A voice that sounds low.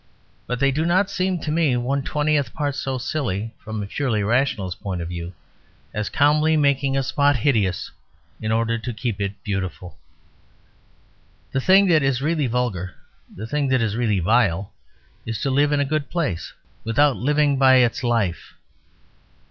Yes: low, 130 Hz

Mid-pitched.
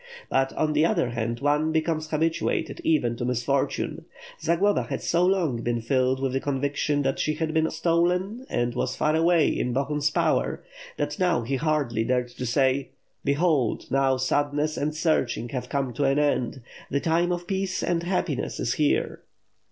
Yes: medium, 145 Hz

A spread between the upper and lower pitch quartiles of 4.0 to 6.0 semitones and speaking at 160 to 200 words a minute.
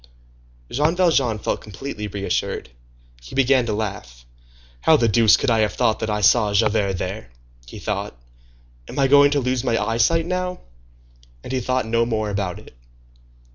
Yes: average, 4.3 semitones; average, 170 wpm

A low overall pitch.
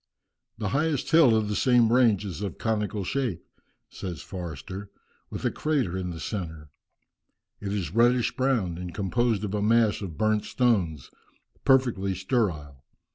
Yes: low, 105 Hz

